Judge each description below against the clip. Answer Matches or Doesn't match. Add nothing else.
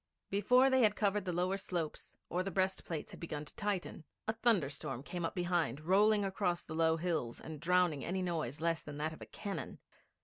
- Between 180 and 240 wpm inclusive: Matches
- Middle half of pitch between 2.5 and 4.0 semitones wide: Matches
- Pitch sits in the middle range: Matches